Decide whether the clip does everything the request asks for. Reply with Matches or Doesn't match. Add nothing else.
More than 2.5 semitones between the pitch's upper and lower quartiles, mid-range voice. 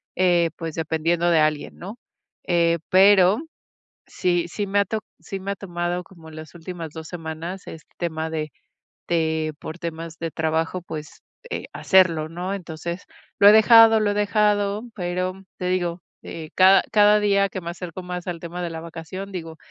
Matches